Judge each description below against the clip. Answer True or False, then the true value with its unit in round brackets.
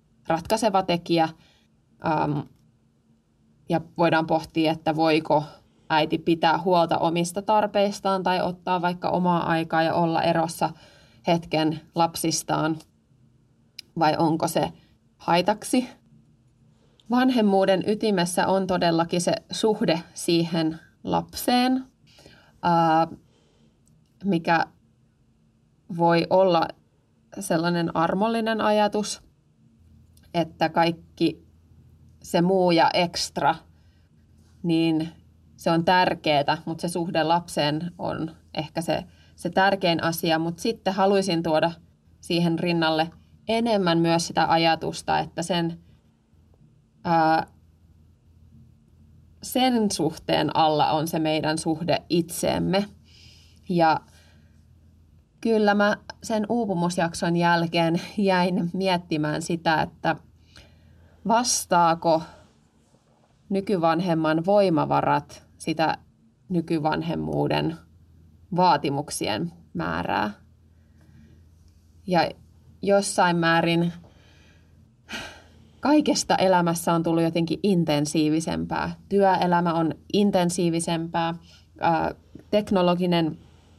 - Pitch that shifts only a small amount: False (3.3 semitones)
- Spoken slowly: True (80 wpm)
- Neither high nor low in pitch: True (165 Hz)